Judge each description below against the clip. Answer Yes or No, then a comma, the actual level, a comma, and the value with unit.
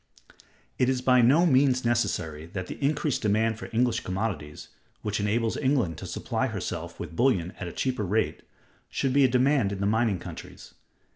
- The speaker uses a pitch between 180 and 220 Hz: No, low, 115 Hz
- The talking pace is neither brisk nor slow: Yes, average, 175 wpm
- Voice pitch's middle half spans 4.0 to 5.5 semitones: Yes, average, 4.7 semitones